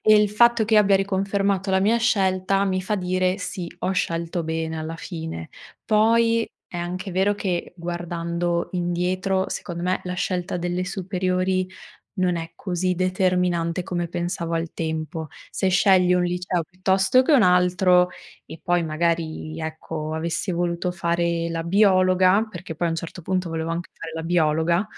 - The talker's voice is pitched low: No, medium, 180 Hz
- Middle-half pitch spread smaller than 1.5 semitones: No, narrow, 2.0 semitones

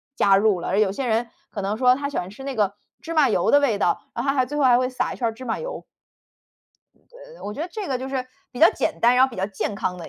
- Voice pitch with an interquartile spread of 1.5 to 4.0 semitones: No, average, 4.8 semitones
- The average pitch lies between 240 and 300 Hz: Yes, very high, 250 Hz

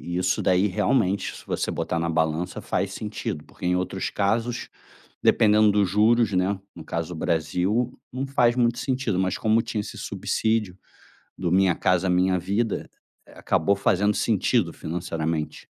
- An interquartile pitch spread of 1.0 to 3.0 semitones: No, average, 3.8 semitones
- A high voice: No, very low, 95 Hz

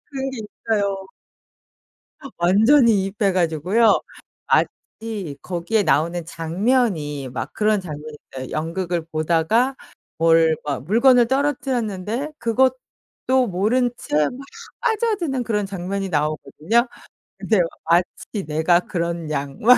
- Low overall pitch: No, high, 195 Hz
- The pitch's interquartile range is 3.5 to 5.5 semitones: No, wide, 6.5 semitones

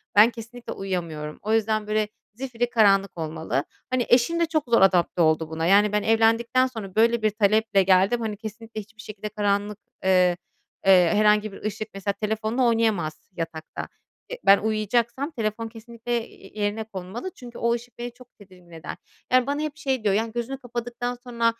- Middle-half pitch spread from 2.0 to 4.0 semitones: Yes, average, 3.3 semitones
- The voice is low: No, high, 220 Hz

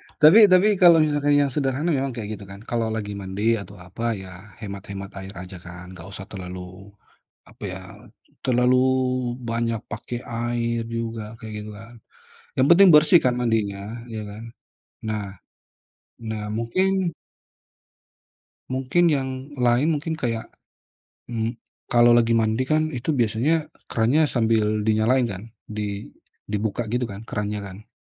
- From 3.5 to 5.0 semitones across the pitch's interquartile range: Yes, average, 3.9 semitones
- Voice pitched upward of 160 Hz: No, low, 115 Hz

